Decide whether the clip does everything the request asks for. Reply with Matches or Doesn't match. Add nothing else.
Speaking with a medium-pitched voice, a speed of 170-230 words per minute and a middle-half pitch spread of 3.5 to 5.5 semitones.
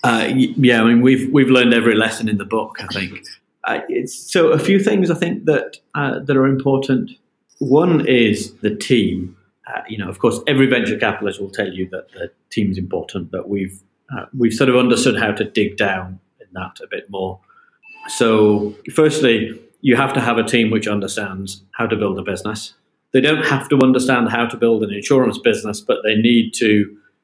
Doesn't match